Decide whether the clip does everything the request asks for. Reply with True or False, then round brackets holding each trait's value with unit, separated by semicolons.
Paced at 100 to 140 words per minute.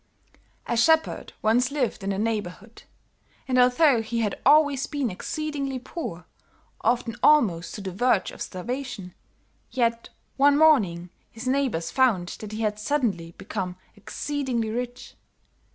True (135 wpm)